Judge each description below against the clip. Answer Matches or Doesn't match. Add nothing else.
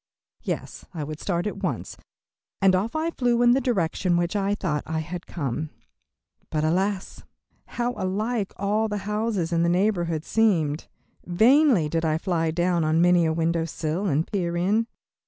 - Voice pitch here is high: Doesn't match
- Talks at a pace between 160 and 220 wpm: Matches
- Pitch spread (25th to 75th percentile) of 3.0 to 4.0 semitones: Doesn't match